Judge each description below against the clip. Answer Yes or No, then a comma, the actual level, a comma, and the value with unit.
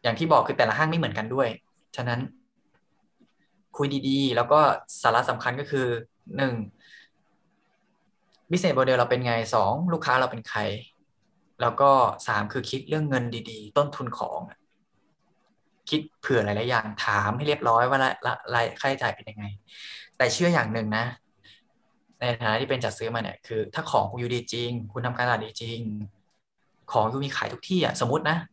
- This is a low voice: Yes, low, 125 Hz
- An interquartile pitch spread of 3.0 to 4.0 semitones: Yes, average, 3.7 semitones